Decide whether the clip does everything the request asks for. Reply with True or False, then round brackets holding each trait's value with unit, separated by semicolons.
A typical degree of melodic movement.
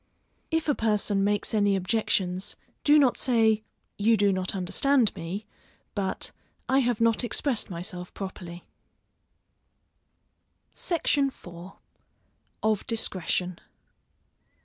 True (4.1 semitones)